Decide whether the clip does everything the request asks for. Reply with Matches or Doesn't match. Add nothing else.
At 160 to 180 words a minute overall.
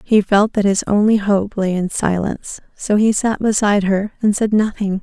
Doesn't match